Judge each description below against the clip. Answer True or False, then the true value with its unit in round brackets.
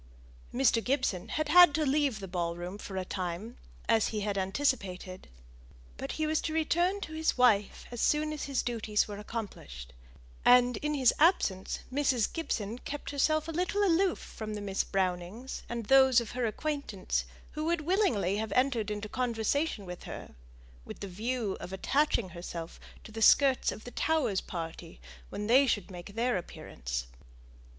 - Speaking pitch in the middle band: False (230 Hz)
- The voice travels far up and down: True (6.7 semitones)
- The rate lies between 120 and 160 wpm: False (170 wpm)